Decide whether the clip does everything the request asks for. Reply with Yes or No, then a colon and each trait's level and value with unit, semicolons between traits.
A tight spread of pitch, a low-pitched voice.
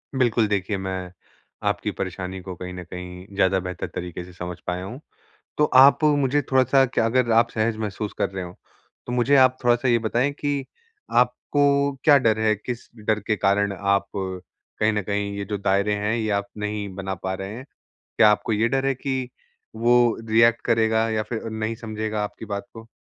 No: average, 3.6 semitones; low, 110 Hz